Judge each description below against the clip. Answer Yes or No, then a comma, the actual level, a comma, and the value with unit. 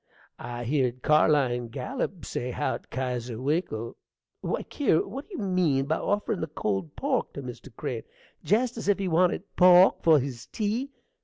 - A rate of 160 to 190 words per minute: Yes, average, 165 wpm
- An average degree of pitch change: No, wide, 7.7 semitones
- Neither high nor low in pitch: Yes, medium, 155 Hz